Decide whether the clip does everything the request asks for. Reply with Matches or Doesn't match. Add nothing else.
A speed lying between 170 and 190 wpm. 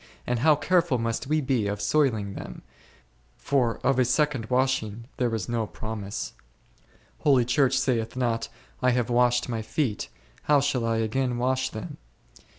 Doesn't match